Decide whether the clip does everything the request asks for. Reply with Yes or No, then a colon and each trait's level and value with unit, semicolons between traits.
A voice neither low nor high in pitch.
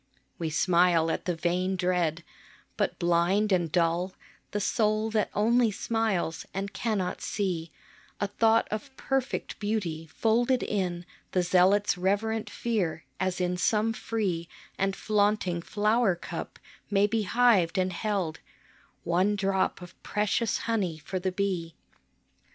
No: high, 195 Hz